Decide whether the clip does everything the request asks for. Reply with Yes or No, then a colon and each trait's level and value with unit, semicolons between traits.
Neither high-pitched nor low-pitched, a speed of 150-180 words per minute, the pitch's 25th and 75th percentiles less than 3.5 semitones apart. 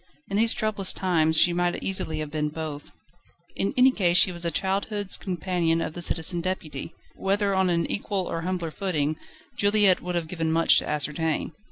No: medium, 175 Hz; average, 190 wpm; average, 3.1 semitones